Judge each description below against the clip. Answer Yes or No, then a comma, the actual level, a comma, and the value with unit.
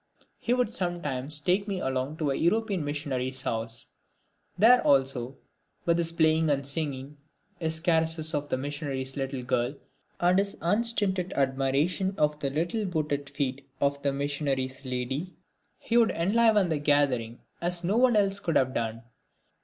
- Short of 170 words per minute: Yes, average, 155 wpm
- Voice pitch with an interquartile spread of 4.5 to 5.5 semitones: Yes, average, 4.9 semitones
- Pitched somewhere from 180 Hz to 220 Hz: No, medium, 150 Hz